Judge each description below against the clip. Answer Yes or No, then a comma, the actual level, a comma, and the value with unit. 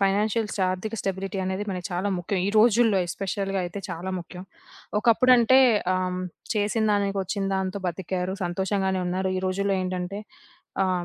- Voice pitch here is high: Yes, high, 195 Hz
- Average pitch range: No, narrow, 1.9 semitones